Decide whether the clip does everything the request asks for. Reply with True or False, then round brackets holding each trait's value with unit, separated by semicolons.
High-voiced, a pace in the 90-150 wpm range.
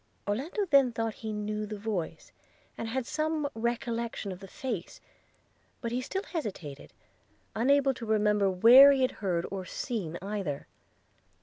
True (225 Hz; 145 wpm)